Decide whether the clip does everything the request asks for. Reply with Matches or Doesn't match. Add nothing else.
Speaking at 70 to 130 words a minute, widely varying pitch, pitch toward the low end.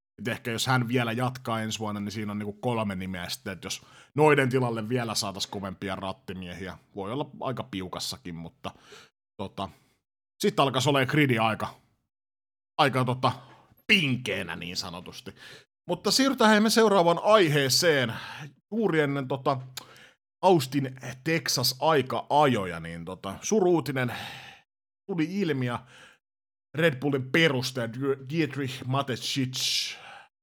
Matches